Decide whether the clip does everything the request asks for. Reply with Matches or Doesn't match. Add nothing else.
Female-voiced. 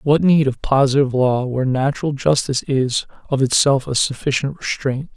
Doesn't match